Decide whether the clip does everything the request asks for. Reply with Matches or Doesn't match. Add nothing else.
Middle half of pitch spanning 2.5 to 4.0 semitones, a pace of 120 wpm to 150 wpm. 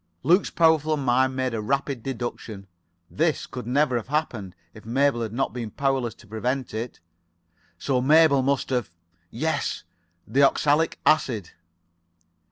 Matches